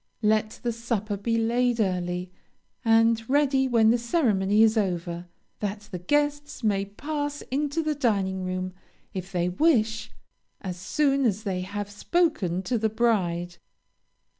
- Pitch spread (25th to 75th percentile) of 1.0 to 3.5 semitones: No, average, 4.8 semitones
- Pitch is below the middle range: No, high, 220 Hz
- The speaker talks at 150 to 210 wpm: No, average, 140 wpm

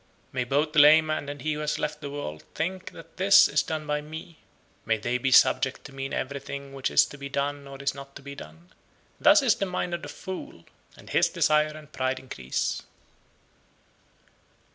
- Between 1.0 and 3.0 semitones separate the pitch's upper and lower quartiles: Yes, narrow, 2.4 semitones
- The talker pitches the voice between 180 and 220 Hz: No, medium, 145 Hz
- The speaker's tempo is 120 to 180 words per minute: No, fast, 205 wpm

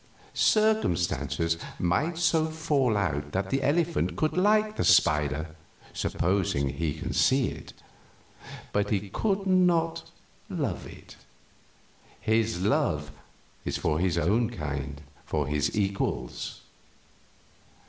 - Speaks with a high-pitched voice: No, low, 100 Hz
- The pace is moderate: No, slow, 110 wpm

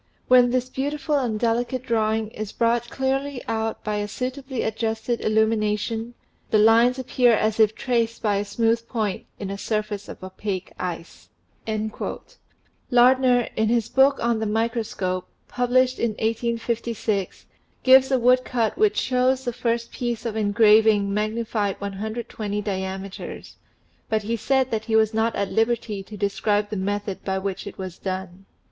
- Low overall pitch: No, high, 225 Hz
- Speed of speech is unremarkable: Yes, average, 160 wpm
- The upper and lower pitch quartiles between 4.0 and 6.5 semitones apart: No, average, 2.8 semitones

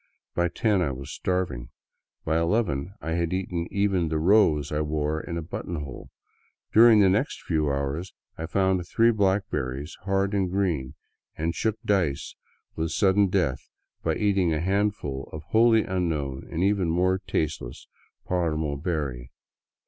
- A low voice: Yes, very low, 85 Hz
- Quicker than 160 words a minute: No, average, 155 wpm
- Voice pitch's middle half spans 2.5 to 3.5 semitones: No, average, 4.3 semitones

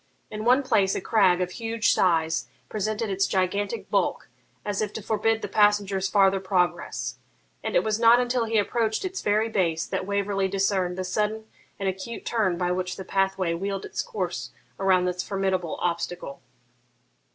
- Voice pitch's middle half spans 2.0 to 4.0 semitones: Yes, average, 2.8 semitones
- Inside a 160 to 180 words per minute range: Yes, average, 170 wpm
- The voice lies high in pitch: Yes, high, 195 Hz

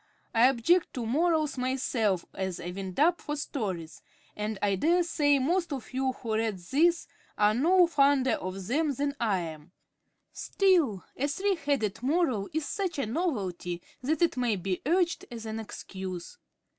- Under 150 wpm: No, average, 165 wpm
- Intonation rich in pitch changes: Yes, wide, 7.8 semitones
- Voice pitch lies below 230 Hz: No, very high, 255 Hz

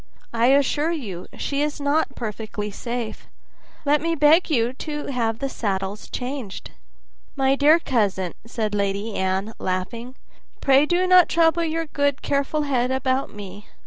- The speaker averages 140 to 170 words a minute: Yes, average, 145 wpm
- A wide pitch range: Yes, wide, 5.7 semitones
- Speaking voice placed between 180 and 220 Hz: No, very high, 260 Hz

